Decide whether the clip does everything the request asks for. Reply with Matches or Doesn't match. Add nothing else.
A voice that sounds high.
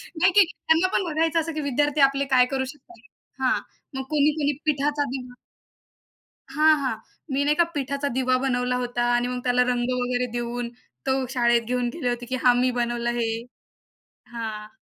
Matches